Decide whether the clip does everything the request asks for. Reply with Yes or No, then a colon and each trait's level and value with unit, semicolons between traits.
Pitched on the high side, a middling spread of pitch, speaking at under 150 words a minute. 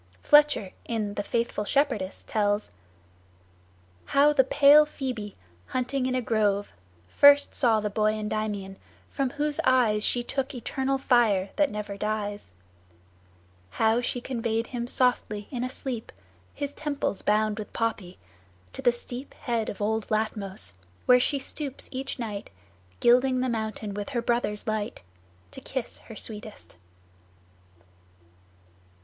Yes: high, 230 Hz; average, 3.7 semitones; slow, 135 wpm